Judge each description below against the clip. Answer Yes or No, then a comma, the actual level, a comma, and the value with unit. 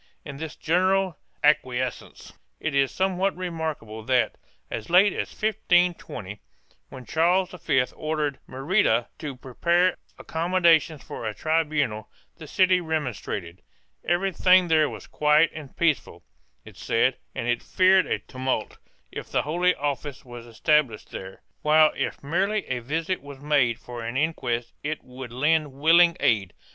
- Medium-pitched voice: Yes, medium, 150 Hz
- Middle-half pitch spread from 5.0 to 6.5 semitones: Yes, average, 5.3 semitones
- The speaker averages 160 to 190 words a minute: No, average, 140 wpm